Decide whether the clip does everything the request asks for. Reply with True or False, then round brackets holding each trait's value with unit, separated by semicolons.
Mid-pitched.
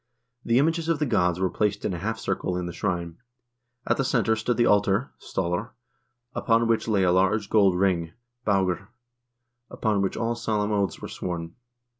False (100 Hz)